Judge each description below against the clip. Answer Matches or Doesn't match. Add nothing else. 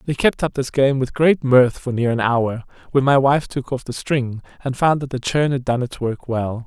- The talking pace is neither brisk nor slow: Doesn't match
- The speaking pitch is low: Matches